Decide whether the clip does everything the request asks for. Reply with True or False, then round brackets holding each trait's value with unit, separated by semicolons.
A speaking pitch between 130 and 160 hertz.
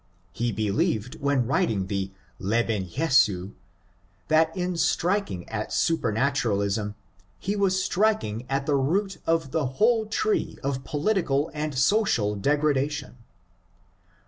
True (140 Hz)